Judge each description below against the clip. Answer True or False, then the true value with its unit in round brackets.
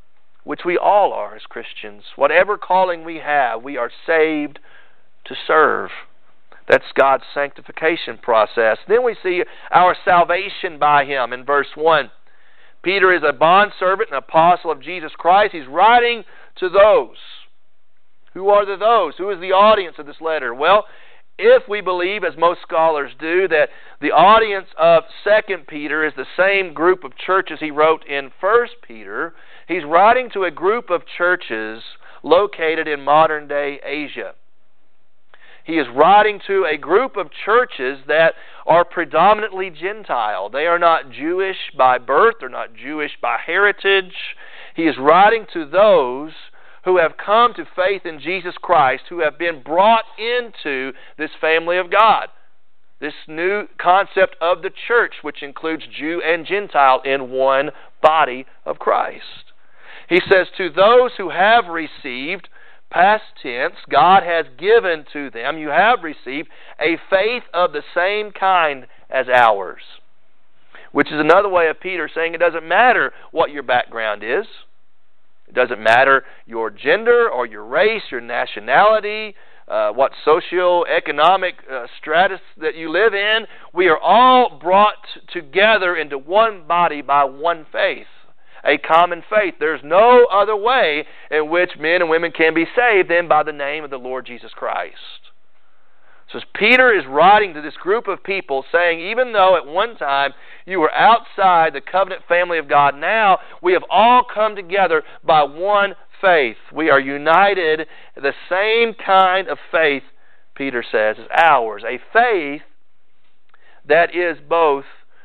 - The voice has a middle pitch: True (175 Hz)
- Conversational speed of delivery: True (155 wpm)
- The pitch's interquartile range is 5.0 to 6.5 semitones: True (5.3 semitones)